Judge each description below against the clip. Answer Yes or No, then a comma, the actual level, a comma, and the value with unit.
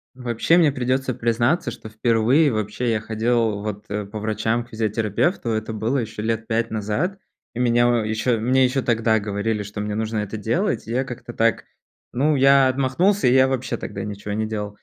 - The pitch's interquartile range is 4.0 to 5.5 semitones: No, average, 2.9 semitones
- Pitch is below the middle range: Yes, low, 115 Hz